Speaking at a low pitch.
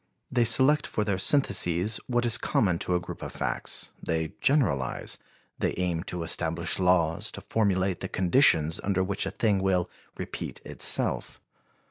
Yes: very low, 95 Hz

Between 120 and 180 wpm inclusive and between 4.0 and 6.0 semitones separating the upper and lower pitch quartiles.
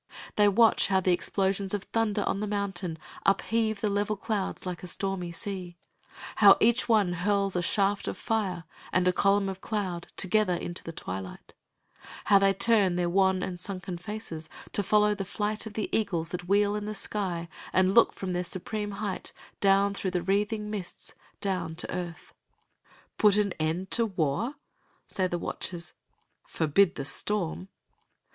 No: average, 170 wpm; narrow, 2.6 semitones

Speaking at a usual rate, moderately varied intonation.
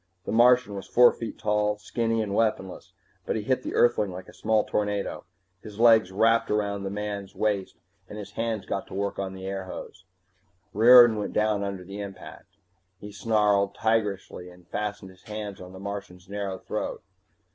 No: average, 180 wpm; narrow, 2.0 semitones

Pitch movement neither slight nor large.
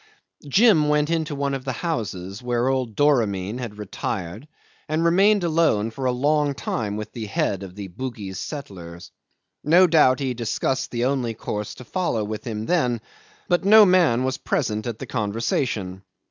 No: wide, 5.9 semitones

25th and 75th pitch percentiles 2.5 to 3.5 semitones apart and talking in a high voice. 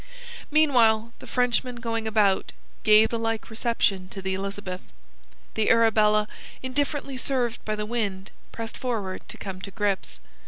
Yes: average, 2.8 semitones; high, 220 Hz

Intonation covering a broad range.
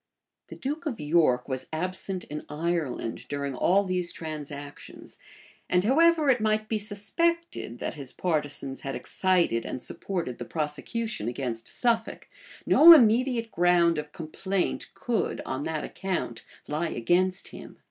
Yes: wide, 6.9 semitones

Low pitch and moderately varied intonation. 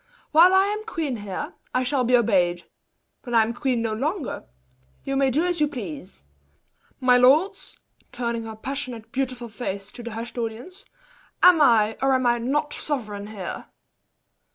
No: high, 245 Hz; average, 4.4 semitones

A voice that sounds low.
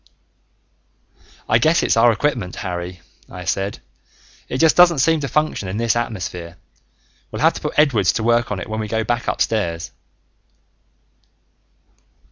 Yes: low, 110 Hz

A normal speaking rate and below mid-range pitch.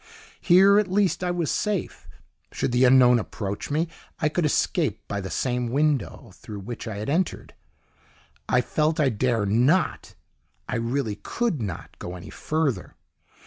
Yes: average, 155 wpm; low, 130 Hz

